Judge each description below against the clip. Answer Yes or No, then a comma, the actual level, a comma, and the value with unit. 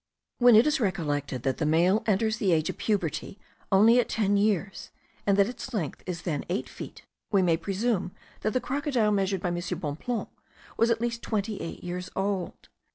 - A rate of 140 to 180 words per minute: No, average, 190 wpm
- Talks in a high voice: Yes, high, 200 Hz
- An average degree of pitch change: Yes, average, 4.2 semitones